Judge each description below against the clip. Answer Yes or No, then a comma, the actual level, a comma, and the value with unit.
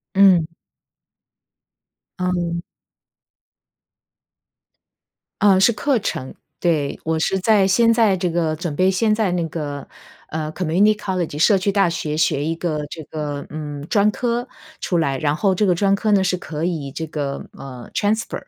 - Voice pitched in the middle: Yes, medium, 175 Hz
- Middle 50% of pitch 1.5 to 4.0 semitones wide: No, average, 4.5 semitones